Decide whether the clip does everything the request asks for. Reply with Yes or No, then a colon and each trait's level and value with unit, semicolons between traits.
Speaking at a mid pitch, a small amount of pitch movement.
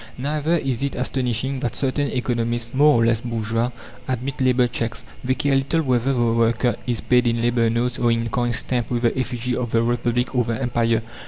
No: low, 120 Hz; narrow, 1.9 semitones